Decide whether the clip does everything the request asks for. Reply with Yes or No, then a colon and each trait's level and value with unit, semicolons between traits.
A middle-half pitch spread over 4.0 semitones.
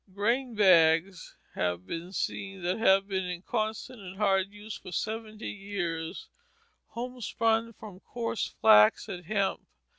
No: average, 3.5 semitones